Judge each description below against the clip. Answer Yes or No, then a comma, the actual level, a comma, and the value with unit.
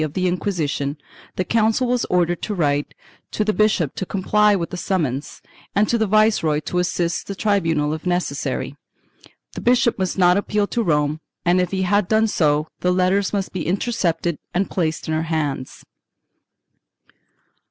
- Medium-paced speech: Yes, average, 170 wpm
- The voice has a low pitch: No, medium, 180 Hz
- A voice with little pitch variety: No, average, 4.4 semitones